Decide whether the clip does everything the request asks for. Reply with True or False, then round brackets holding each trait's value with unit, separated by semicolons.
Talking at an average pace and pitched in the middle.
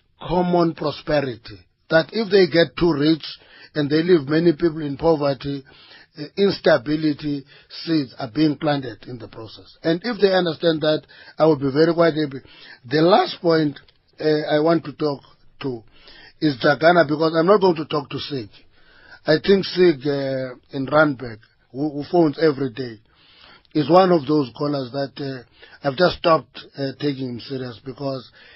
True (165 wpm; 150 Hz)